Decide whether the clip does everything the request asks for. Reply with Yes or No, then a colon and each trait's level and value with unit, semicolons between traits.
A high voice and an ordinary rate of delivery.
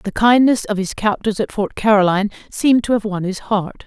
No: high, 210 Hz; fast, 215 wpm